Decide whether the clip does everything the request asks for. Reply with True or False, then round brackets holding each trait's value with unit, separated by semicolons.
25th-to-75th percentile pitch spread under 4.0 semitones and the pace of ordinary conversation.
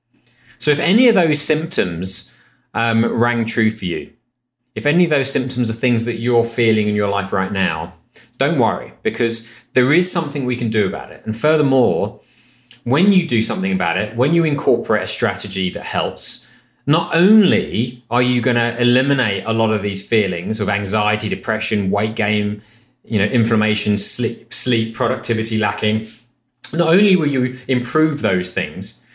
True (3.3 semitones; 170 wpm)